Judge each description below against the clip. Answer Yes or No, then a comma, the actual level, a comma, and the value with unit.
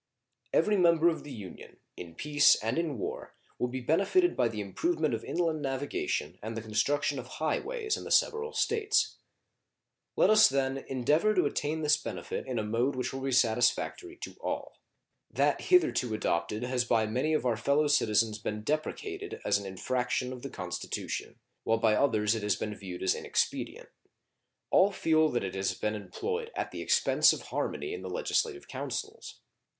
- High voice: No, low, 135 Hz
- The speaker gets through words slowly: No, average, 180 wpm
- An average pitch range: No, wide, 8.8 semitones